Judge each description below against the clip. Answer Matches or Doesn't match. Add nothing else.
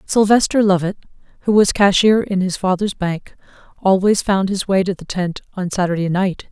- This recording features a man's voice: Doesn't match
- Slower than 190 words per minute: Matches